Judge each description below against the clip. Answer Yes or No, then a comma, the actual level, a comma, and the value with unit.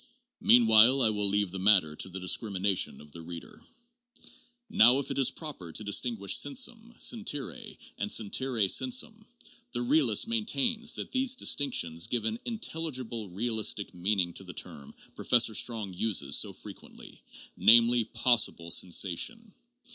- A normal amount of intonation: No, wide, 7.9 semitones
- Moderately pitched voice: No, low, 115 Hz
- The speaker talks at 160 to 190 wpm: No, average, 145 wpm